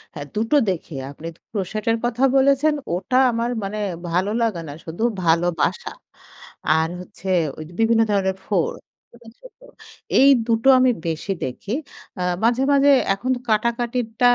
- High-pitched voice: Yes, high, 220 Hz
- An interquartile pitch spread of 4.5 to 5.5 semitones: Yes, average, 5.1 semitones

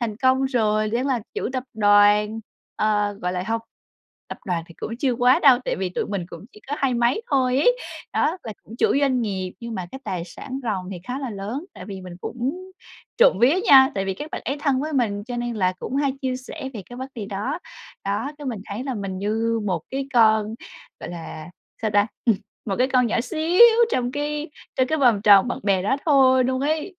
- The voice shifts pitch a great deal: No, average, 4.6 semitones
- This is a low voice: No, high, 235 Hz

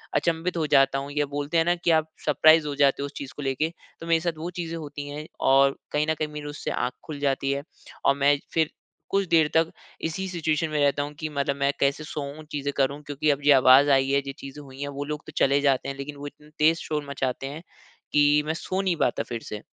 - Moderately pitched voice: Yes, medium, 145 Hz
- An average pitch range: No, narrow, 2.2 semitones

